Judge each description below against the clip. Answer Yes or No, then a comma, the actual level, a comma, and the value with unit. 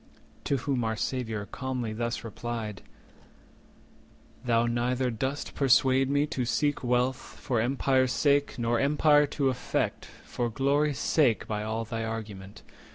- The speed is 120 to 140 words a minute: Yes, slow, 135 wpm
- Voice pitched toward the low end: Yes, low, 125 Hz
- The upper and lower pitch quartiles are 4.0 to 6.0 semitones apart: No, average, 3.1 semitones